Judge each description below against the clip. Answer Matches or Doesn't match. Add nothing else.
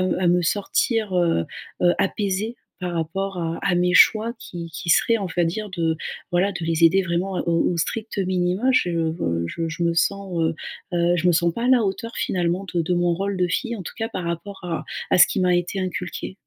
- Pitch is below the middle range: Doesn't match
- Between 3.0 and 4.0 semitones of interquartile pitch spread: Doesn't match